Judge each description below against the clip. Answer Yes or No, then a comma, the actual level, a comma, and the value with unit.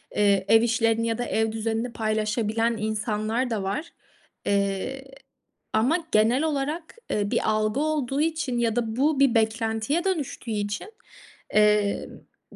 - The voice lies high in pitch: Yes, high, 225 Hz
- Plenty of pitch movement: No, average, 3.9 semitones